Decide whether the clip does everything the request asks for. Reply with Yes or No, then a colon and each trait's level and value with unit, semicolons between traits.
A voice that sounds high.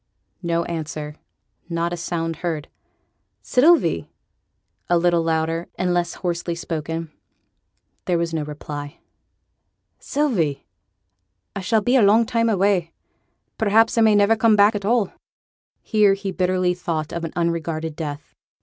No: medium, 175 Hz